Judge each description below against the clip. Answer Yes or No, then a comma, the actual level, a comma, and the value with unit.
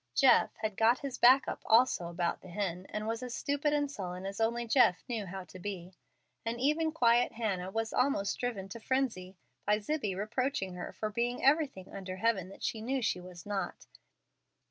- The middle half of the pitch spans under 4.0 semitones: No, average, 4.9 semitones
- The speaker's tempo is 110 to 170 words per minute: No, average, 190 wpm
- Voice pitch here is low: No, high, 220 Hz